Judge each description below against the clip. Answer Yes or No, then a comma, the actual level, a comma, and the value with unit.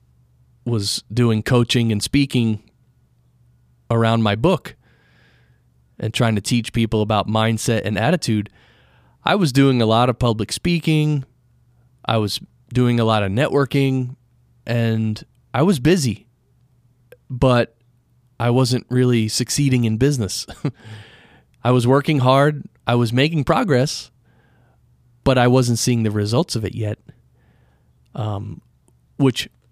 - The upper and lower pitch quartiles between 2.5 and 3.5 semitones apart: Yes, average, 2.9 semitones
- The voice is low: Yes, low, 120 Hz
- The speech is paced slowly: Yes, slow, 125 wpm